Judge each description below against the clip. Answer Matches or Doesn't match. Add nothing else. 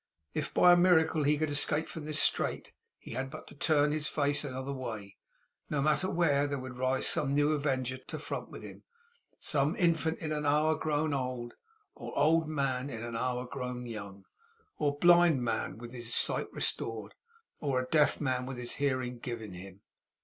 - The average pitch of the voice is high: Doesn't match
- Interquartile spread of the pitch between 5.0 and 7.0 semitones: Doesn't match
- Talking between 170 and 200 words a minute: Matches